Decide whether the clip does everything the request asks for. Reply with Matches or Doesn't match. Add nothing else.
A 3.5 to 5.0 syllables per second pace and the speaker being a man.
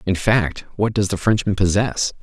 Matches